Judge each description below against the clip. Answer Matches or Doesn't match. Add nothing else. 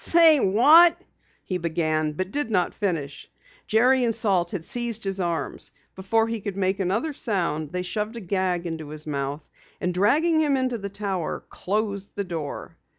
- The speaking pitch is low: Doesn't match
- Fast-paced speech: Doesn't match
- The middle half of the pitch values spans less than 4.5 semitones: Doesn't match